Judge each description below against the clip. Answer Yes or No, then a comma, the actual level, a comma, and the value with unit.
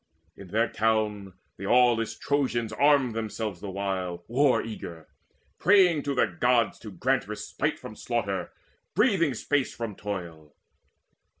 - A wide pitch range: No, average, 5.0 semitones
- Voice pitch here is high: No, low, 115 Hz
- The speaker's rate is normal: No, slow, 130 wpm